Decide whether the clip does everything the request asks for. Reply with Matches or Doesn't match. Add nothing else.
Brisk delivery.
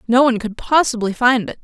Matches